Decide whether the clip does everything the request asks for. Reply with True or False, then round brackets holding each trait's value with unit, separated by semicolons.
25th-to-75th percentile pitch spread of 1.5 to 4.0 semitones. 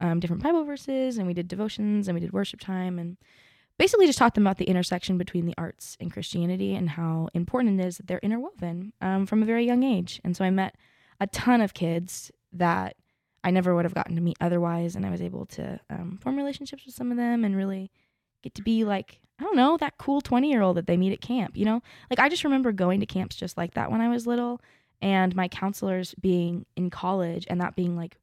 False (5.1 semitones)